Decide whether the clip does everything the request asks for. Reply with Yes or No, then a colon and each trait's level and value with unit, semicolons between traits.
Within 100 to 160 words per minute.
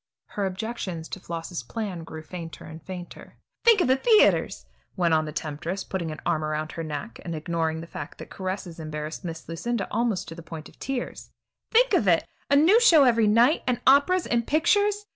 No: average, 200 wpm